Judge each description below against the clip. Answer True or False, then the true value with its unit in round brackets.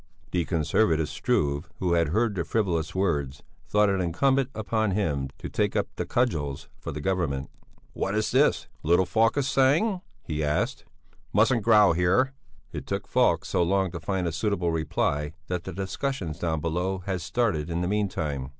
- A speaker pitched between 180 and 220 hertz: False (90 Hz)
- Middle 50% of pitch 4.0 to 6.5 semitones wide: True (4.9 semitones)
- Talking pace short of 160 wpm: False (175 wpm)